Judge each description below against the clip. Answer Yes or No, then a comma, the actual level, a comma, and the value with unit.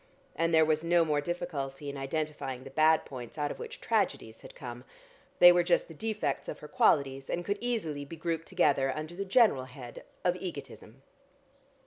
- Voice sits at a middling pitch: Yes, medium, 155 Hz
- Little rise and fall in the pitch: No, average, 4.1 semitones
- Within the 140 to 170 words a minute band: No, average, 185 wpm